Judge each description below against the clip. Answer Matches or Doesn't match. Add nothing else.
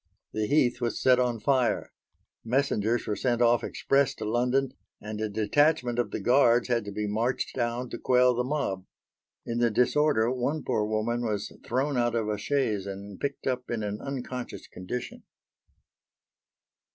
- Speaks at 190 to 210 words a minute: Doesn't match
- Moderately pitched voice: Doesn't match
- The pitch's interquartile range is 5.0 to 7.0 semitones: Doesn't match